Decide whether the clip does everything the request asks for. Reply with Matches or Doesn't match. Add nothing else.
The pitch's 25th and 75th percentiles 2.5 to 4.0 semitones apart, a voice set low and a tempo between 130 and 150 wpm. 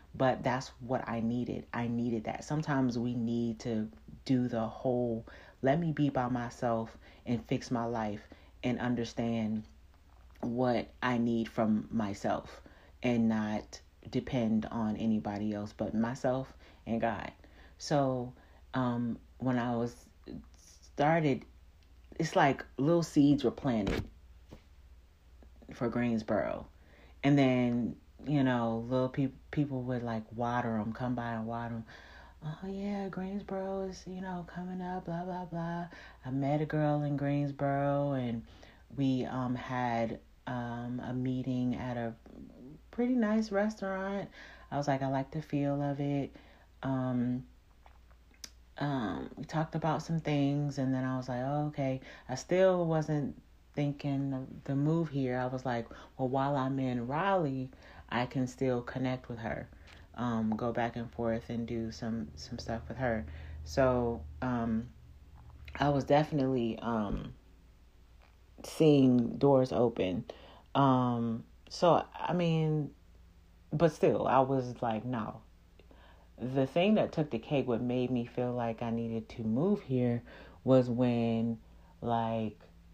Matches